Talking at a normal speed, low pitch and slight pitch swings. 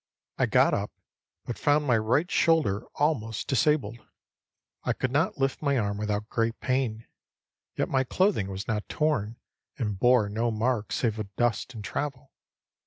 No: average, 160 wpm; low, 120 Hz; average, 4.5 semitones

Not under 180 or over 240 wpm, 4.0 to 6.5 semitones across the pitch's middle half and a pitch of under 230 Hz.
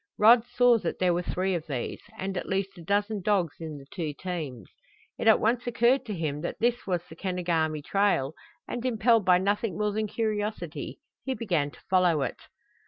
Yes: average, 195 wpm; average, 4.7 semitones; high, 190 Hz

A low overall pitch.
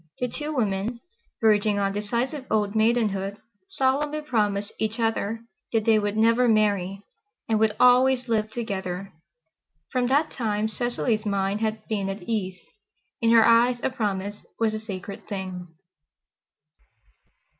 No: high, 220 Hz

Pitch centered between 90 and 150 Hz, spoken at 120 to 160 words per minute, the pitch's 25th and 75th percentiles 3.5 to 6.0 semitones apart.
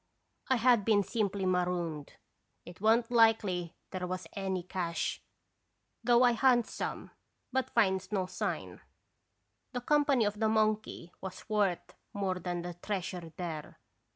No: high, 200 Hz; average, 140 wpm; average, 4.0 semitones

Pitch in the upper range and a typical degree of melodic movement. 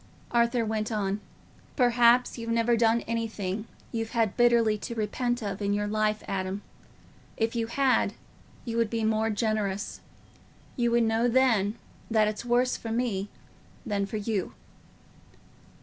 No: high, 225 Hz; narrow, 2.0 semitones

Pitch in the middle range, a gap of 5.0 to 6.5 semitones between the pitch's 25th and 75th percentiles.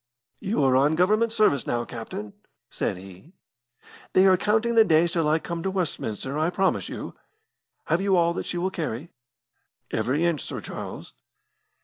Yes: medium, 170 Hz; wide, 5.4 semitones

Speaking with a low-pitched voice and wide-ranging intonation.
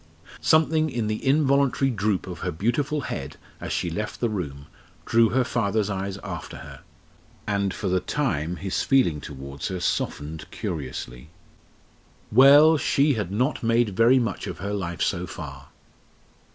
Yes: low, 105 Hz; wide, 6.9 semitones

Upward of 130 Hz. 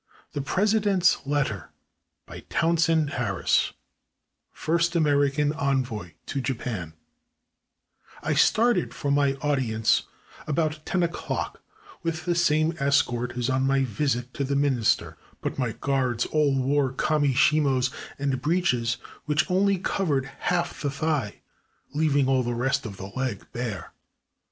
Yes: medium, 140 Hz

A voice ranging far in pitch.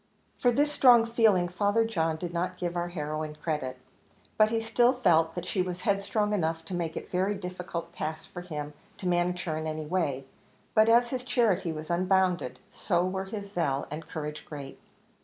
No: average, 4.3 semitones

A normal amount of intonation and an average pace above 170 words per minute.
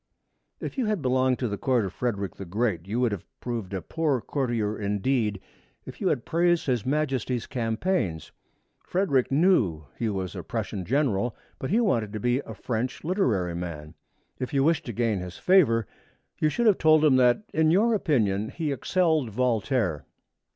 No: wide, 6.9 semitones; average, 180 wpm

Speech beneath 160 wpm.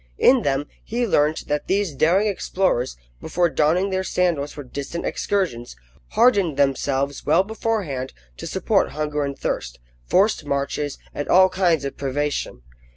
Yes: average, 145 wpm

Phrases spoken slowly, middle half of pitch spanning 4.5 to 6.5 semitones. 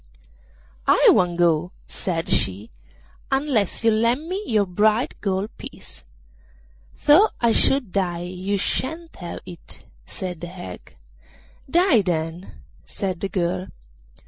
Yes: slow, 120 wpm; average, 5.1 semitones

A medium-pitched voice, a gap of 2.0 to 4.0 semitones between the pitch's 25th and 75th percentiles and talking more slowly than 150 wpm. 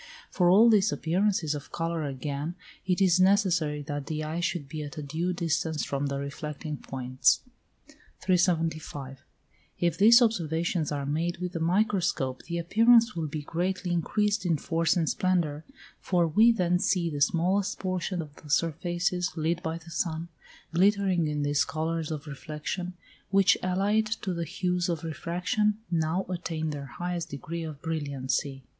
No: medium, 170 Hz; average, 3.2 semitones; average, 160 wpm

